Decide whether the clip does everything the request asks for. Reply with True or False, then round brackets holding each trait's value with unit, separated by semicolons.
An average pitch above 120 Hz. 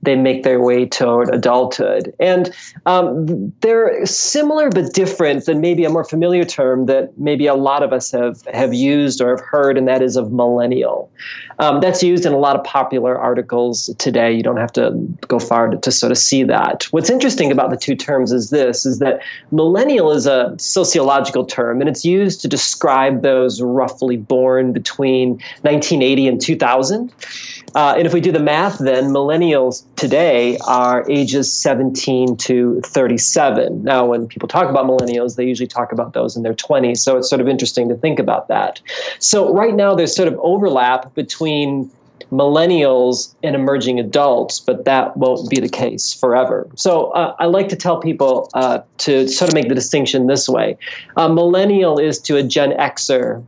True (135 Hz)